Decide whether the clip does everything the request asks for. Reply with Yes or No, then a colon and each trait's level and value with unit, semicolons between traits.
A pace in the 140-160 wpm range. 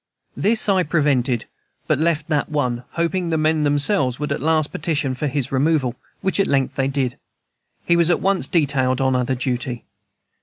No: average, 180 wpm